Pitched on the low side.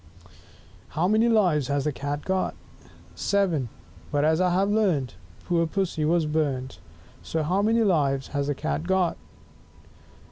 No: medium, 160 Hz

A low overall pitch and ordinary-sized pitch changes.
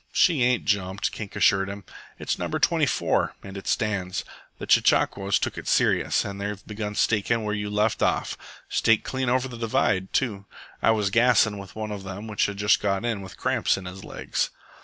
No: low, 105 Hz; narrow, 2.3 semitones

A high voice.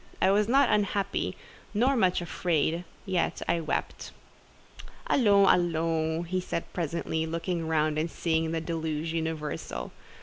No: medium, 165 Hz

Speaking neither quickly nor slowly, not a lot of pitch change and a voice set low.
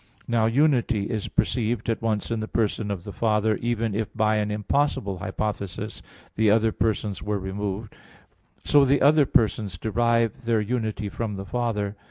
Yes: average, 165 wpm; narrow, 2.1 semitones; low, 110 Hz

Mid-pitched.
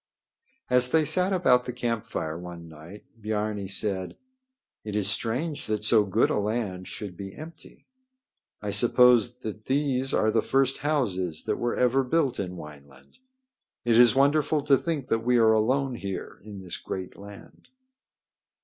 No: low, 115 Hz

